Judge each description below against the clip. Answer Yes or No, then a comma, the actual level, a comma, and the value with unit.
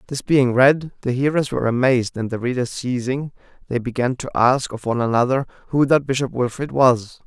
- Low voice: Yes, low, 130 Hz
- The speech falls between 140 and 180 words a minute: No, average, 190 wpm